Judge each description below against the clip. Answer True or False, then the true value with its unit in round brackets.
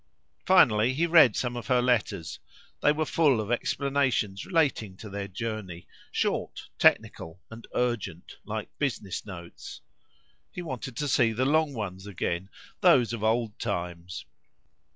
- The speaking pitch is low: True (115 Hz)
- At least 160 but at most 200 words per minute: False (140 wpm)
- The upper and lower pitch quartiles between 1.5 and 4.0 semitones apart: False (5.3 semitones)